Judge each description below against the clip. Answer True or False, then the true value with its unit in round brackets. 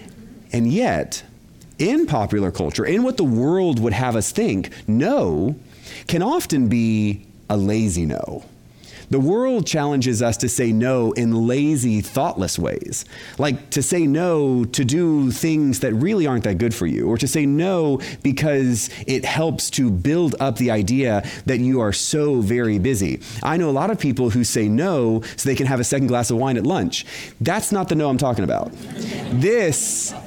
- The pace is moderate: True (180 wpm)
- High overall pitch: False (130 Hz)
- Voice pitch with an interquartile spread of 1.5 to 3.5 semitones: False (4.0 semitones)